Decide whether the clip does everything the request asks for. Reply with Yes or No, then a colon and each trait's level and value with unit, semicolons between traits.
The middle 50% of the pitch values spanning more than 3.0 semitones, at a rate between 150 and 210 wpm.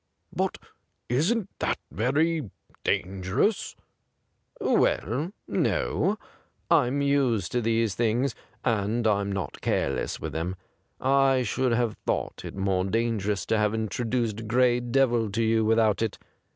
No: average, 3.4 semitones; slow, 135 wpm